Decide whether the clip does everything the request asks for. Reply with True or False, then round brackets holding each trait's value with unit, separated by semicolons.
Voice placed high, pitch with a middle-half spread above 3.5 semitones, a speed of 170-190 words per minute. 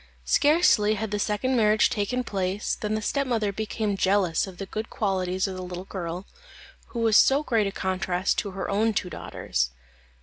False (205 Hz; 2.7 semitones; 180 wpm)